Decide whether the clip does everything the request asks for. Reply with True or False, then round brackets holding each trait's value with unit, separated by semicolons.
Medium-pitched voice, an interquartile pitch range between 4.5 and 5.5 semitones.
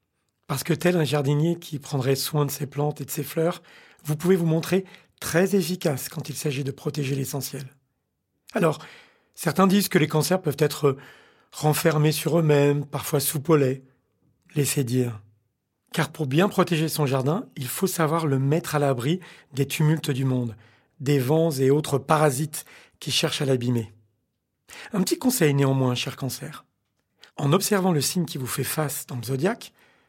False (150 Hz; 3.3 semitones)